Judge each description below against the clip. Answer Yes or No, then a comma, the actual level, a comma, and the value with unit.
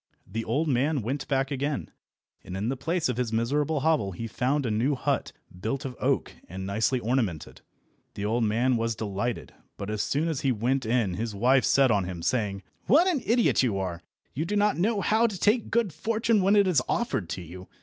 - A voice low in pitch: Yes, low, 125 Hz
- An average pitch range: No, wide, 6.9 semitones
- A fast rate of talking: Yes, fast, 210 wpm